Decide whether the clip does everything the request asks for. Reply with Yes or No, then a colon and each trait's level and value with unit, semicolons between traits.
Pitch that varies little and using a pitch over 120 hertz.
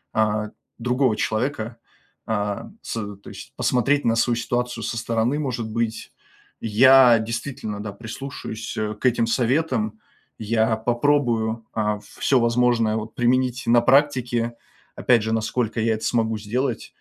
No: narrow, 2.1 semitones; low, 115 Hz